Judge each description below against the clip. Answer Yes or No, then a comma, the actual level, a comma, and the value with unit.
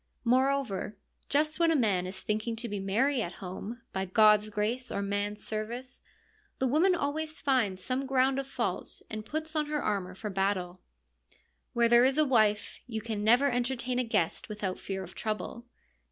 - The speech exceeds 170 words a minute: Yes, average, 185 wpm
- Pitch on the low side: No, high, 230 Hz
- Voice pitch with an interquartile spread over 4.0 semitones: Yes, average, 4.6 semitones